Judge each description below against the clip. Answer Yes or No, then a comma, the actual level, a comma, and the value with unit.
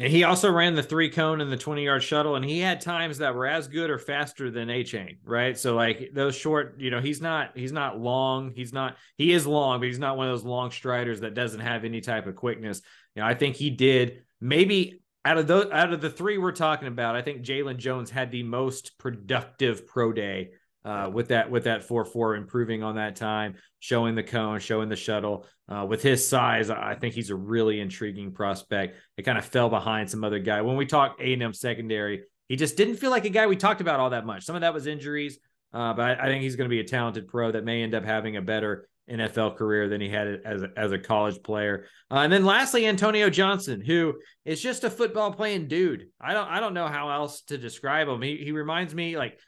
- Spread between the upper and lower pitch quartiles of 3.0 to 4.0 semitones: No, average, 5.2 semitones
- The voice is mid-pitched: No, low, 125 Hz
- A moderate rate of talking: No, fast, 245 wpm